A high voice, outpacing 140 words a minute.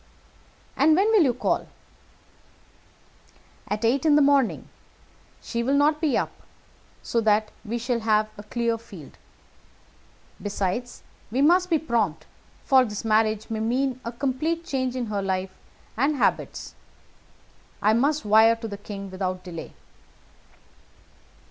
No: high, 235 Hz; slow, 135 wpm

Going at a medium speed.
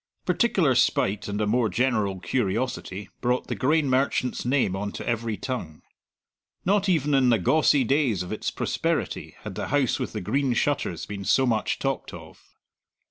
Yes: average, 170 wpm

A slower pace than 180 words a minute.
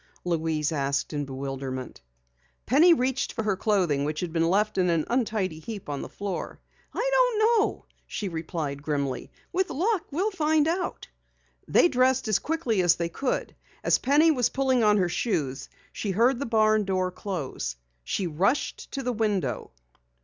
Yes: average, 165 wpm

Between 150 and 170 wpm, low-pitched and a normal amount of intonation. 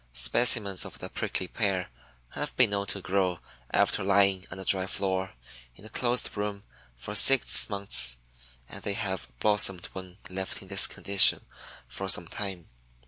No: average, 160 wpm; very low, 95 Hz; narrow, 1.5 semitones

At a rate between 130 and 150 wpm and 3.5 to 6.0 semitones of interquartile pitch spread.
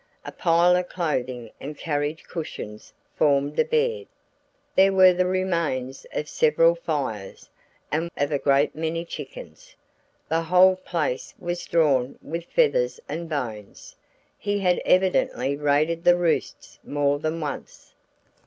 Yes: slow, 135 wpm; average, 4.0 semitones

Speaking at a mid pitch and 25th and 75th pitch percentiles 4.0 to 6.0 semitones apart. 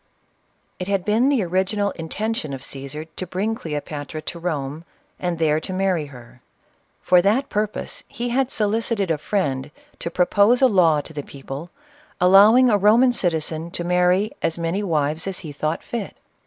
Yes: medium, 180 Hz; average, 5.1 semitones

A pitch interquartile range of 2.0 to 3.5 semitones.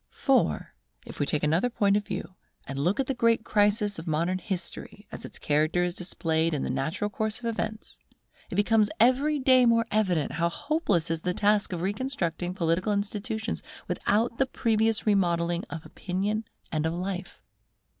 No: average, 4.5 semitones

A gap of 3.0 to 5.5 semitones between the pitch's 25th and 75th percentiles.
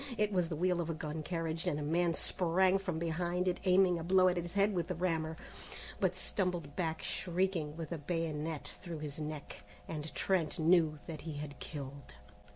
No: narrow, 2.6 semitones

